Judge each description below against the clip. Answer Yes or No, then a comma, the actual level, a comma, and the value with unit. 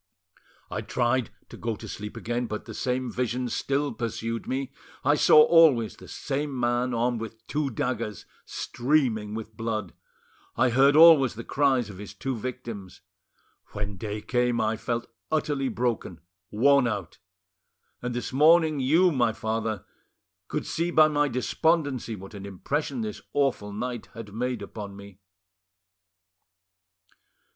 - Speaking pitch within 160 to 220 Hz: No, low, 120 Hz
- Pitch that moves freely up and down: No, average, 4.1 semitones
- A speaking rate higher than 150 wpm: No, average, 145 wpm